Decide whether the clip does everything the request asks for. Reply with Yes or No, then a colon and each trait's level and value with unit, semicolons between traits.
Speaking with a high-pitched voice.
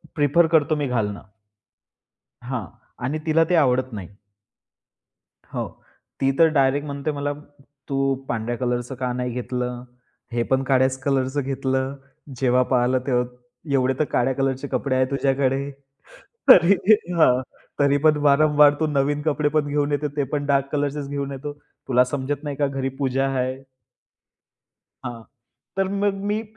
No: low, 135 Hz